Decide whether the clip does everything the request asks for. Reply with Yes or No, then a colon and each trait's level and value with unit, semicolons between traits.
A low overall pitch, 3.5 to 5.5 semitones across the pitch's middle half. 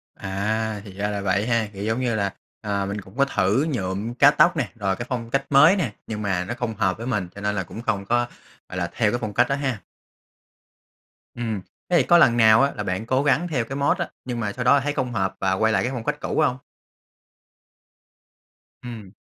Yes: low, 115 Hz; average, 4.4 semitones